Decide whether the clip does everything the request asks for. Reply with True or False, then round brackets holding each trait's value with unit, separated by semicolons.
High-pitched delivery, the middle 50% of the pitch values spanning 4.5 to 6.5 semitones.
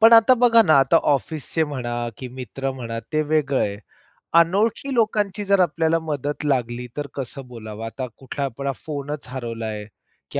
False (145 Hz; 4.9 semitones)